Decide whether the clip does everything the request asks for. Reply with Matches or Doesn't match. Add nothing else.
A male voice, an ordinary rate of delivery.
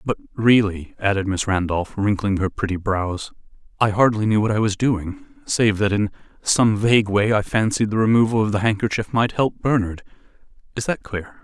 Matches